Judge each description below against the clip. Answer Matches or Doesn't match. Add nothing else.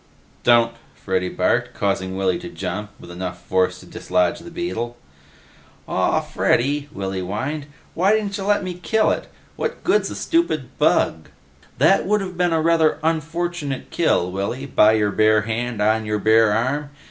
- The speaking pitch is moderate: Doesn't match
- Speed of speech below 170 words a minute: Matches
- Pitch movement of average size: Doesn't match